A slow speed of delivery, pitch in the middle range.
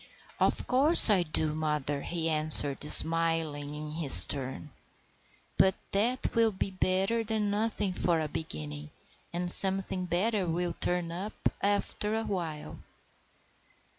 Yes: slow, 130 wpm; medium, 175 Hz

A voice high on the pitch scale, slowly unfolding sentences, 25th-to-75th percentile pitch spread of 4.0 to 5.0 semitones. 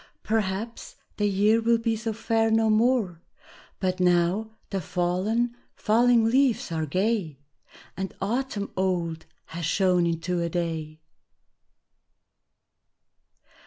Yes: high, 200 Hz; slow, 110 wpm; average, 4.4 semitones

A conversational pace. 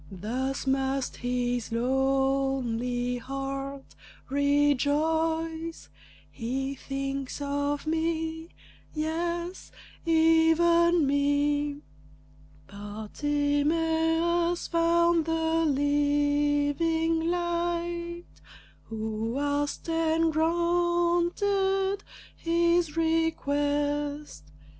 No: slow, 60 wpm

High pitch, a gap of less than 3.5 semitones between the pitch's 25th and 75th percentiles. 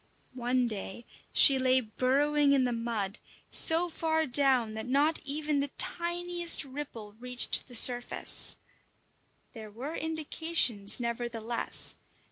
No: very high, 260 Hz; average, 4.4 semitones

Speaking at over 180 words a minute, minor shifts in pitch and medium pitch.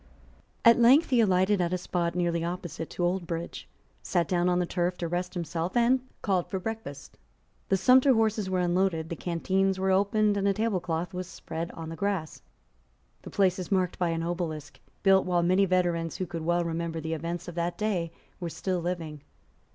Yes: average, 190 wpm; narrow, 2.3 semitones; medium, 180 Hz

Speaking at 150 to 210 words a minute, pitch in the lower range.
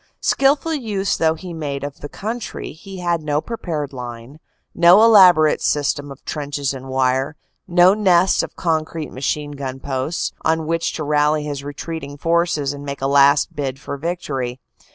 No: average, 165 wpm; medium, 150 Hz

